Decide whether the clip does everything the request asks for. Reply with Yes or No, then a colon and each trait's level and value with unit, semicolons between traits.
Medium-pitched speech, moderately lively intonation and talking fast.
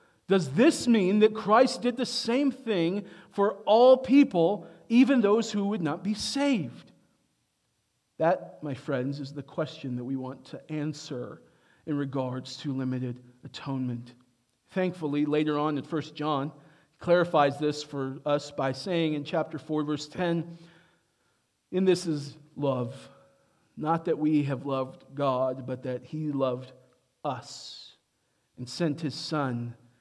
No: medium, 150 Hz; average, 4.8 semitones; average, 145 wpm